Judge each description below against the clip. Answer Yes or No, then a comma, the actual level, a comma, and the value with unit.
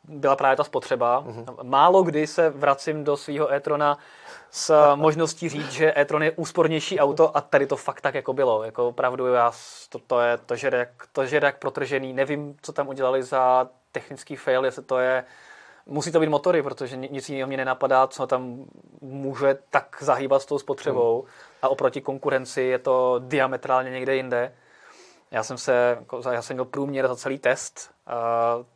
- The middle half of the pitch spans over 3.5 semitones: No, narrow, 2.5 semitones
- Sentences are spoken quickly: Yes, fast, 175 wpm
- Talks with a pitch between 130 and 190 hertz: Yes, low, 135 Hz